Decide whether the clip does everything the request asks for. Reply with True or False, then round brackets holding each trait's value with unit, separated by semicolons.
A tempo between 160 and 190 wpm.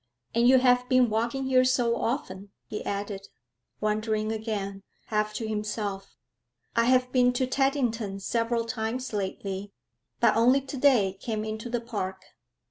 False (140 wpm)